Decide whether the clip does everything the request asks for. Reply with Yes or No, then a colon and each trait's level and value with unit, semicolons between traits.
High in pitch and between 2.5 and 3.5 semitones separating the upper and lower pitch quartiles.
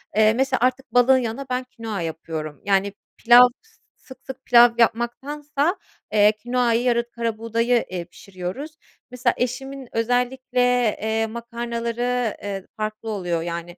Yes: high, 235 Hz; average, 2.8 semitones